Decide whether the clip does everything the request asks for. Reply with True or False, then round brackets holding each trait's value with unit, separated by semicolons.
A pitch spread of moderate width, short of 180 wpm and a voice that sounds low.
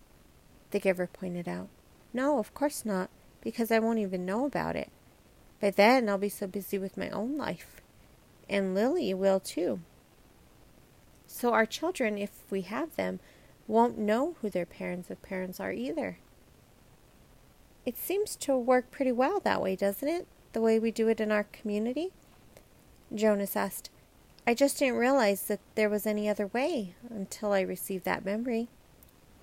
False (4.3 semitones; 165 wpm; 215 Hz)